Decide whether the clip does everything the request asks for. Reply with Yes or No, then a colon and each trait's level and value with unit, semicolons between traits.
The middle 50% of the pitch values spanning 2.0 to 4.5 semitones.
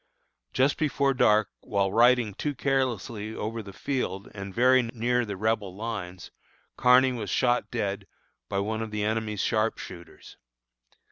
Yes: average, 3.5 semitones